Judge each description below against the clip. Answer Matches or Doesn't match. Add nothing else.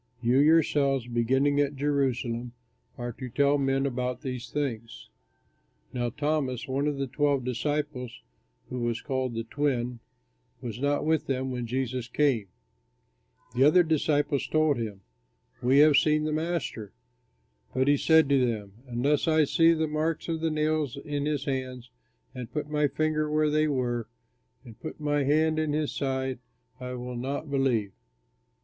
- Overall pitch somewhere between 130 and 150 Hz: Matches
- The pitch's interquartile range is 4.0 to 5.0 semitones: Doesn't match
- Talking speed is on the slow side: Doesn't match